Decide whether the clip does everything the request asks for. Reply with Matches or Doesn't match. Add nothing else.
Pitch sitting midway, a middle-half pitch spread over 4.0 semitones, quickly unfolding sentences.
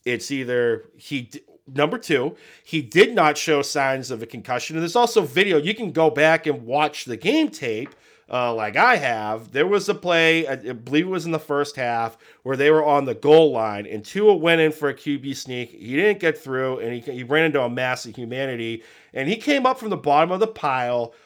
Matches